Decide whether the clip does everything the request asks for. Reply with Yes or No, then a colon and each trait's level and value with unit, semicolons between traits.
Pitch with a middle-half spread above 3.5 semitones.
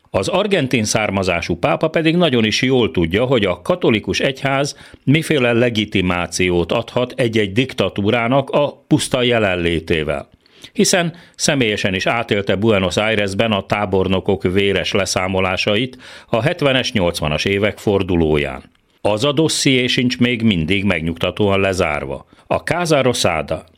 Yes: wide, 5.6 semitones